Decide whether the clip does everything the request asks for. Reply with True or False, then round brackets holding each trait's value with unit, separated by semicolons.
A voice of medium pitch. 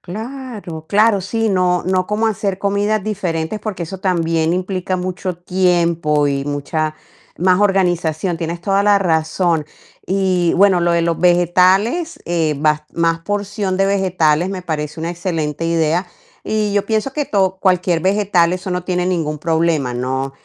True (180 Hz)